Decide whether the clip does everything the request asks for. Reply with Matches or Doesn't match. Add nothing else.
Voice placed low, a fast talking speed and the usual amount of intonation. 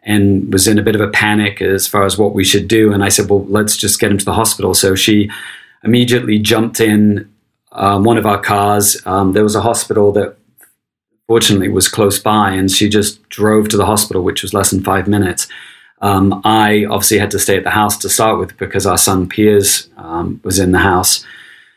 Doesn't match